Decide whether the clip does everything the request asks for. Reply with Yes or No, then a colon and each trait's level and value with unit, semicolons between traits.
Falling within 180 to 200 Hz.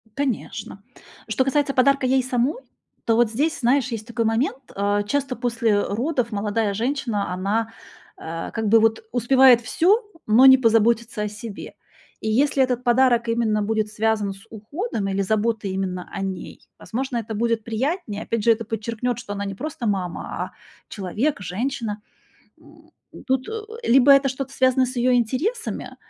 No: high, 230 Hz